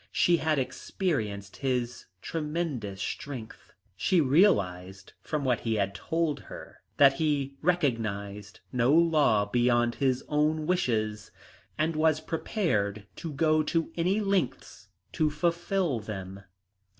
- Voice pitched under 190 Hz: Yes, medium, 140 Hz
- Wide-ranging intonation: Yes, wide, 7.1 semitones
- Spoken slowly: Yes, slow, 120 wpm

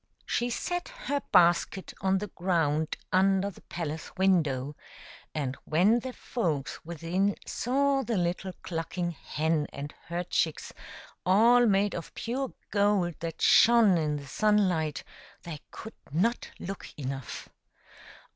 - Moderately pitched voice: Yes, medium, 180 Hz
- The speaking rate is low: Yes, slow, 130 wpm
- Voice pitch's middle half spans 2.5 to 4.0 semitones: No, average, 4.8 semitones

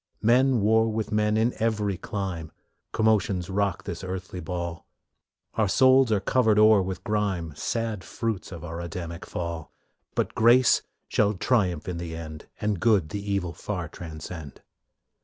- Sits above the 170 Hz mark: No, low, 100 Hz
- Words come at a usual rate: Yes, average, 150 wpm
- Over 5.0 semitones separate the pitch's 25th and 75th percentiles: No, average, 4.1 semitones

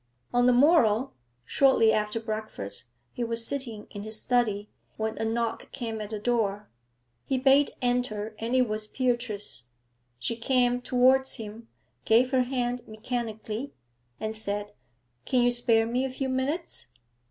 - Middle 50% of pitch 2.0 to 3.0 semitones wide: Yes, narrow, 2.6 semitones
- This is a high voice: Yes, high, 235 Hz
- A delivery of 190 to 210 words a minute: No, average, 150 wpm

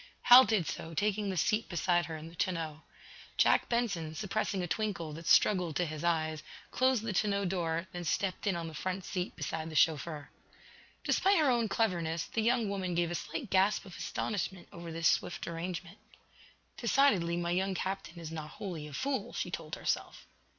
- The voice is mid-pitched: Yes, medium, 180 Hz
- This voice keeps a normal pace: Yes, average, 185 wpm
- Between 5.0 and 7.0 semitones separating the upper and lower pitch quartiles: No, average, 3.8 semitones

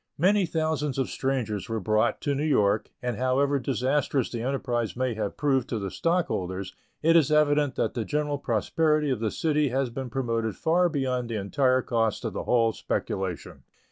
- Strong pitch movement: No, average, 4.5 semitones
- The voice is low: Yes, low, 130 Hz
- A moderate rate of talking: Yes, average, 180 wpm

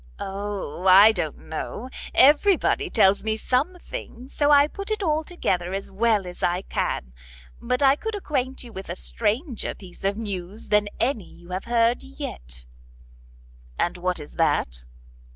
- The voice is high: Yes, high, 220 Hz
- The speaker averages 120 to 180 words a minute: Yes, average, 155 wpm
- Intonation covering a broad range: Yes, wide, 6.6 semitones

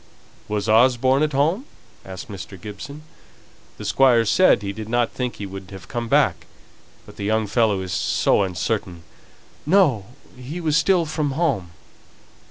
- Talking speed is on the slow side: No, average, 160 wpm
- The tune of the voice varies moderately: No, wide, 6.2 semitones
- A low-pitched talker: Yes, low, 115 Hz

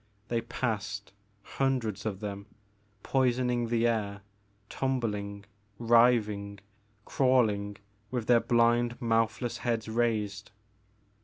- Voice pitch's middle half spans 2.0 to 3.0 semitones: Yes, average, 2.7 semitones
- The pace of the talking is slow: Yes, slow, 95 wpm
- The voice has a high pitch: No, low, 115 Hz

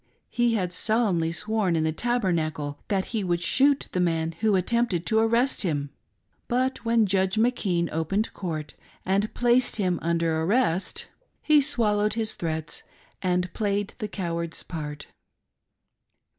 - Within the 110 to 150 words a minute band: Yes, average, 140 wpm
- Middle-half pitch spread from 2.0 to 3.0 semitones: No, average, 5.1 semitones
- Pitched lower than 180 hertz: No, high, 190 Hz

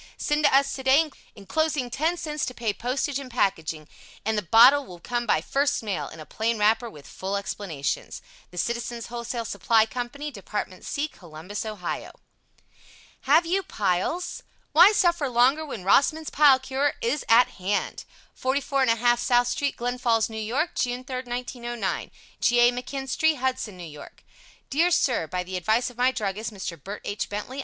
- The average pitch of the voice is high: Yes, high, 240 Hz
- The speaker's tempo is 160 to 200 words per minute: Yes, average, 165 wpm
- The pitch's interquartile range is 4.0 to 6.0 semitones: Yes, average, 4.9 semitones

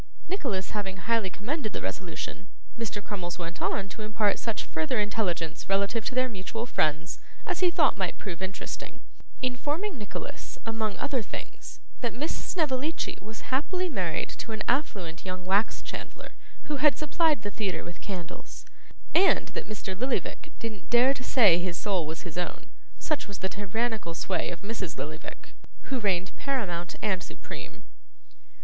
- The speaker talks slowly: No, average, 160 wpm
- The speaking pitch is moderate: No, high, 210 Hz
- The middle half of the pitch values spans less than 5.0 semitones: No, wide, 5.4 semitones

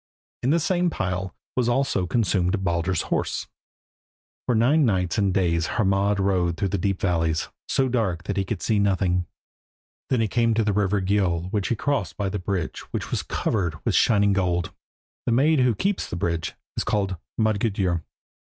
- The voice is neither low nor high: No, low, 100 Hz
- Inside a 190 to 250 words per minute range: No, average, 175 wpm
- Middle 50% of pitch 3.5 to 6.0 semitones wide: Yes, average, 4.0 semitones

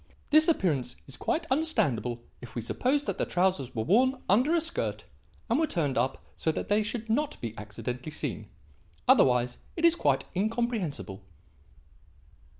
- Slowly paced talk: No, average, 155 wpm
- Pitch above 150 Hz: Yes, high, 190 Hz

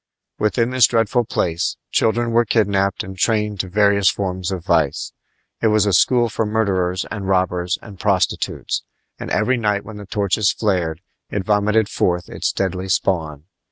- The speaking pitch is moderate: No, low, 100 Hz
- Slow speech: No, average, 160 wpm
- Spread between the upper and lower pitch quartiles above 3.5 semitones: No, average, 2.8 semitones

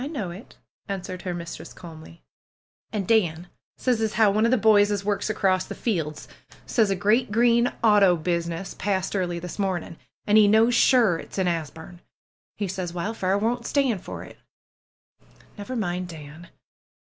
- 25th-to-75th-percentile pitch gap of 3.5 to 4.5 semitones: Yes, average, 4.0 semitones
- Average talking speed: Yes, average, 170 wpm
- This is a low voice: No, high, 195 Hz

